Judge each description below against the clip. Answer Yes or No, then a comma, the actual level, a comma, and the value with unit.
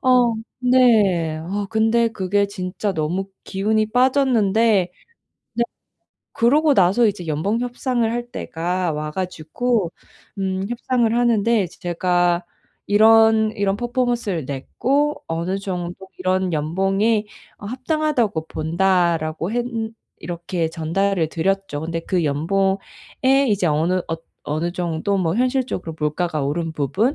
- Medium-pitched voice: No, high, 195 Hz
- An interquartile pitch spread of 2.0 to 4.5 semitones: No, average, 5.3 semitones